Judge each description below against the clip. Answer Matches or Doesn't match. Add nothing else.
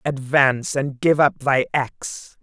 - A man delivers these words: Matches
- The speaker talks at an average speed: Matches